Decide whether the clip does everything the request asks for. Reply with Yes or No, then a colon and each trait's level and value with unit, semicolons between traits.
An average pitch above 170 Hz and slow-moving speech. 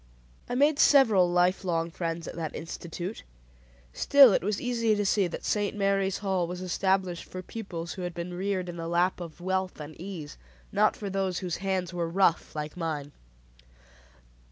No: medium, 185 Hz; average, 180 wpm